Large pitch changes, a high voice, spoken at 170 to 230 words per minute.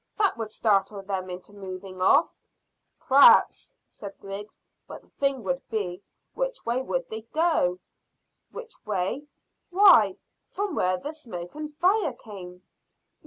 No: wide, 8.1 semitones; high, 215 Hz; slow, 135 wpm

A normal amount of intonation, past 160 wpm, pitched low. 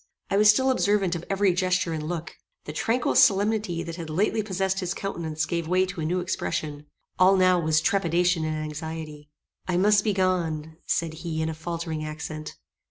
No: average, 3.3 semitones; average, 185 wpm; medium, 175 Hz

